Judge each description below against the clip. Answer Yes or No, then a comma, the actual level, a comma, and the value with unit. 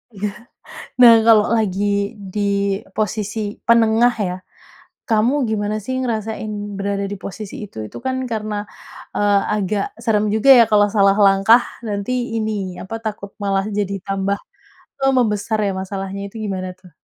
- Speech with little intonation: Yes, narrow, 1.9 semitones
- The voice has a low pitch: No, high, 205 Hz